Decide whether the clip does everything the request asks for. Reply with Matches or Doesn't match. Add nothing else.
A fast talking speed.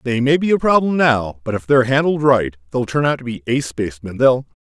Matches